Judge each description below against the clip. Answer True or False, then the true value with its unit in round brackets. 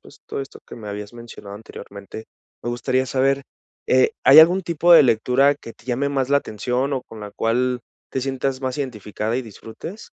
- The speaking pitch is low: True (125 Hz)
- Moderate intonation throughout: True (3.4 semitones)